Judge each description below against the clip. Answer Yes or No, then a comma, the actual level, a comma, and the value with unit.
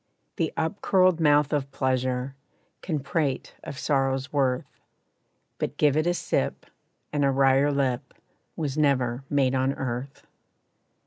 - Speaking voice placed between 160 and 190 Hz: No, medium, 140 Hz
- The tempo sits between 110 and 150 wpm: Yes, slow, 135 wpm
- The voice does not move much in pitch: Yes, narrow, 2.2 semitones